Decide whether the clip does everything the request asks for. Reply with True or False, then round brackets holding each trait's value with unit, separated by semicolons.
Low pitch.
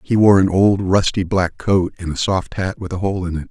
True (95 Hz)